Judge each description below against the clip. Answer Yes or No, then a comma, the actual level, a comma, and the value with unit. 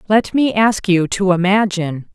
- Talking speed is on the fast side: No, average, 170 wpm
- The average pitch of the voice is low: No, high, 195 Hz